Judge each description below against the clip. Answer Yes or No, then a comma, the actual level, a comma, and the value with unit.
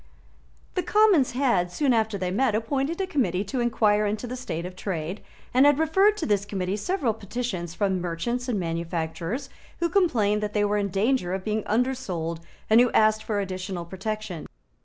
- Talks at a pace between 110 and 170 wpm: No, average, 180 wpm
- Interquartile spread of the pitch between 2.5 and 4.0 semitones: No, wide, 5.5 semitones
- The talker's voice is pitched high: Yes, high, 215 Hz